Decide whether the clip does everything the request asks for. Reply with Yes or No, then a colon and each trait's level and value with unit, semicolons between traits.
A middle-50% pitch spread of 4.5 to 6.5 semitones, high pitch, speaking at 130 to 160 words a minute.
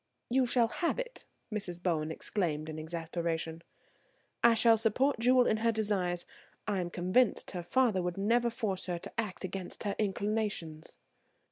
Yes: average, 4.8 semitones; high, 200 Hz; average, 155 wpm